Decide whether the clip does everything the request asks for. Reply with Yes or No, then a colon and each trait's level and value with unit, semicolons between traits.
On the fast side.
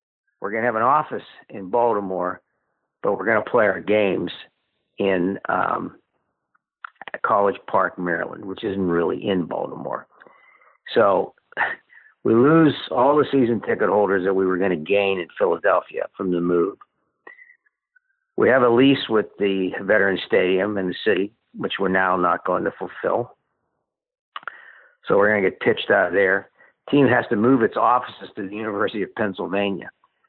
No: average, 165 wpm